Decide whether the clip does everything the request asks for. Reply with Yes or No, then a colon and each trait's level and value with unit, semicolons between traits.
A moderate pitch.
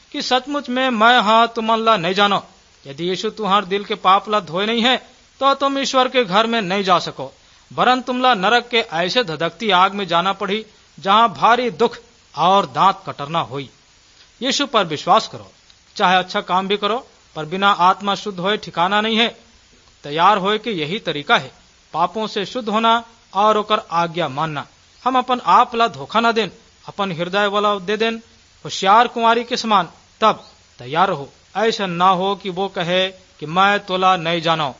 No: high, 205 Hz